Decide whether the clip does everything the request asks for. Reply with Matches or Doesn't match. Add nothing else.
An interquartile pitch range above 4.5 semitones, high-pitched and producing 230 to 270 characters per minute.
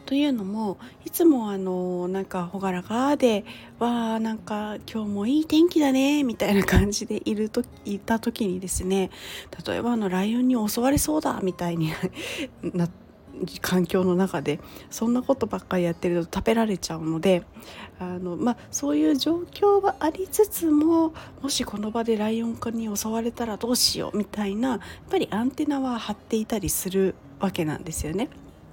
Doesn't match